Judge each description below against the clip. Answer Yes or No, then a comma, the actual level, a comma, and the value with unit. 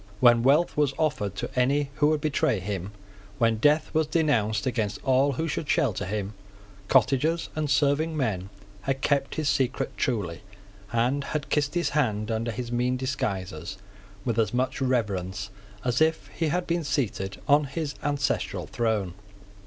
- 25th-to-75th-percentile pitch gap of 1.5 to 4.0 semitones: No, average, 5.3 semitones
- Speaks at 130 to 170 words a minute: Yes, average, 160 wpm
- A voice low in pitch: Yes, low, 130 Hz